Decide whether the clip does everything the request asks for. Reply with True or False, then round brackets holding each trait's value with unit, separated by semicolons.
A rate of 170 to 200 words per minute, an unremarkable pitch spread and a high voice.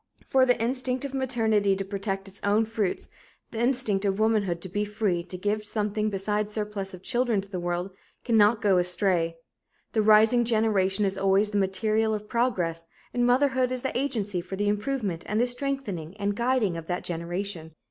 True (185 wpm; 3.4 semitones; 210 Hz)